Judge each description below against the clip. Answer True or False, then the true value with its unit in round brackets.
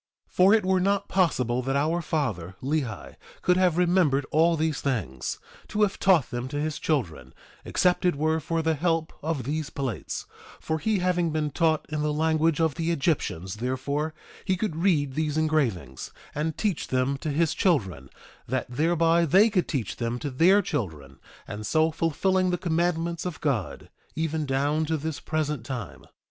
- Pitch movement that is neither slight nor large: True (4.1 semitones)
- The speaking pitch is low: False (155 Hz)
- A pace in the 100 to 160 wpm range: False (175 wpm)